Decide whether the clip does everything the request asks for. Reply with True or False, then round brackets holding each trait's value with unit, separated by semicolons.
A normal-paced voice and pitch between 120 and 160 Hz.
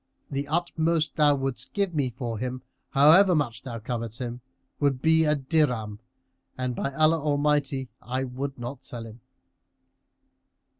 True (145 wpm; 135 Hz)